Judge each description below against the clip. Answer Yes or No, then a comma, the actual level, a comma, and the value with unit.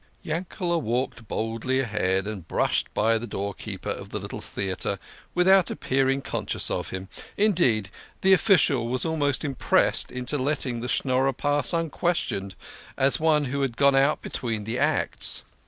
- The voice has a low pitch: Yes, low, 130 Hz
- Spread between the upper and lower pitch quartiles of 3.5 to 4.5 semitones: No, average, 5.1 semitones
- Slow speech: No, average, 155 wpm